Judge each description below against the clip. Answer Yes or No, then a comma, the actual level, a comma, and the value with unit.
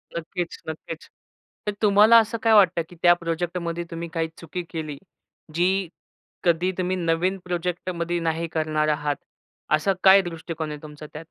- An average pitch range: No, narrow, 2.1 semitones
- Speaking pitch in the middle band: Yes, medium, 170 Hz